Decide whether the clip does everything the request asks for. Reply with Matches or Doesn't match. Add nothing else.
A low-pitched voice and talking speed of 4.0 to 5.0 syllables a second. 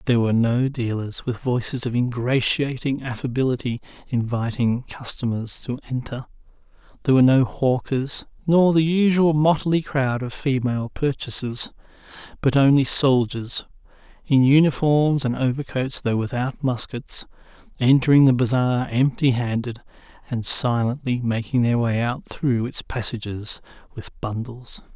Matches